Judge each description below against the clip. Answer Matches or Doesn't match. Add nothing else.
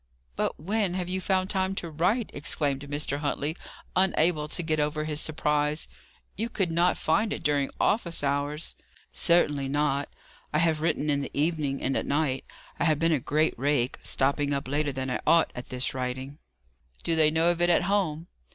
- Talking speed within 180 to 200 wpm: Matches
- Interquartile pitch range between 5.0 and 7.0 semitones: Doesn't match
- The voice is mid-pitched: Matches